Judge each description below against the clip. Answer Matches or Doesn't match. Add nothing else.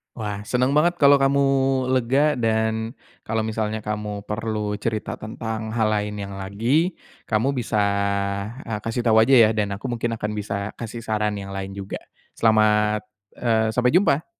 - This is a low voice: Matches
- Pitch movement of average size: Doesn't match